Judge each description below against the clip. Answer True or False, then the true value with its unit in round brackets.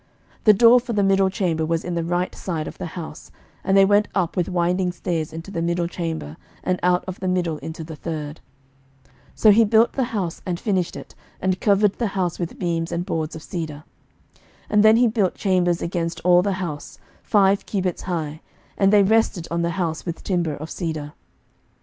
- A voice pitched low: False (180 Hz)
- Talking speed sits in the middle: False (210 wpm)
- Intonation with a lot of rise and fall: False (2.8 semitones)